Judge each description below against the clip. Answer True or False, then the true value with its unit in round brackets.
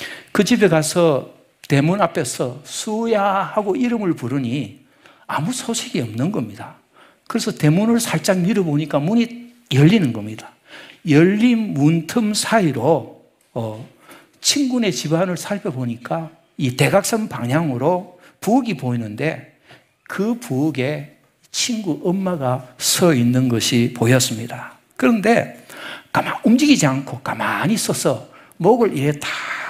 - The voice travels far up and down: True (7.9 semitones)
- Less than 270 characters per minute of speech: True (255 characters per minute)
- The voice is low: False (165 Hz)